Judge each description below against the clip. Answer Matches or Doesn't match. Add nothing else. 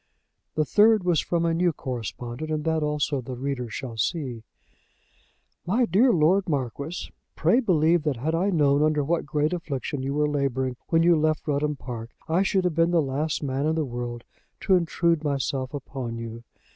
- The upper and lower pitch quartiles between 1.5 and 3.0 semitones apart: Doesn't match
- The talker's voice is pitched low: Doesn't match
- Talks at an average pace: Matches